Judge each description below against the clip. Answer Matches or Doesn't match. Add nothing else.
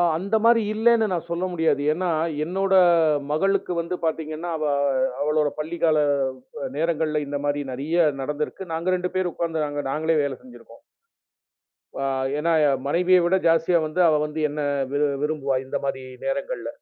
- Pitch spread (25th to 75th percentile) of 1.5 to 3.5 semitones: Matches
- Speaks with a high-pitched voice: Doesn't match